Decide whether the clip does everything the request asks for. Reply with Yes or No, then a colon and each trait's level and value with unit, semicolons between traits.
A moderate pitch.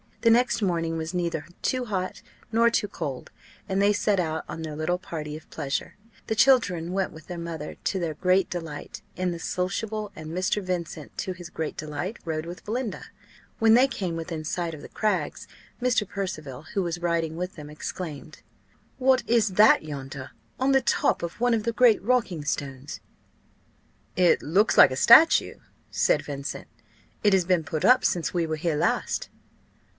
Yes: medium, 175 Hz